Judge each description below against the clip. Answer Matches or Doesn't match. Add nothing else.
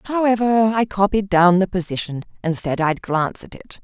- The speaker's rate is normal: Matches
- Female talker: Matches